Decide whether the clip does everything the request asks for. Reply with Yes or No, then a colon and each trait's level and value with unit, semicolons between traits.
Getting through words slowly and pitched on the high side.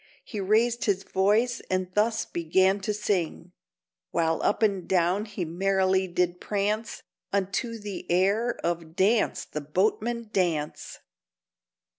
Yes: slow, 125 wpm; high, 195 Hz